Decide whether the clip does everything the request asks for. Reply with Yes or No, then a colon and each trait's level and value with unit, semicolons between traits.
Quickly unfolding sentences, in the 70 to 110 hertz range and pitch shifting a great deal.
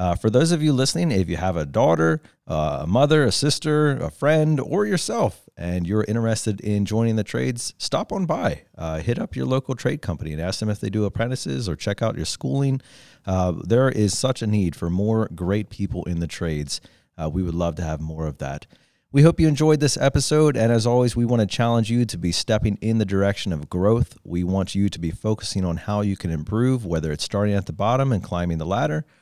Yes: fast, 235 wpm; low, 105 Hz; wide, 6.7 semitones